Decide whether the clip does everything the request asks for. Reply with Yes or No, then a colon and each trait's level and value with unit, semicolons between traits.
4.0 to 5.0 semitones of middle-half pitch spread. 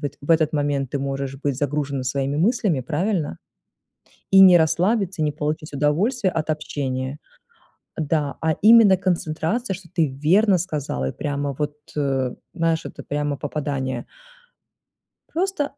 Yes: average, 4.3 semitones